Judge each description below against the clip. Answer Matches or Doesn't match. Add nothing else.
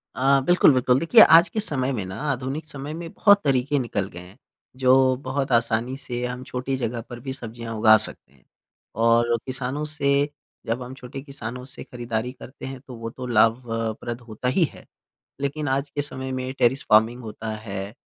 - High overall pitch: Doesn't match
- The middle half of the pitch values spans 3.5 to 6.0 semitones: Doesn't match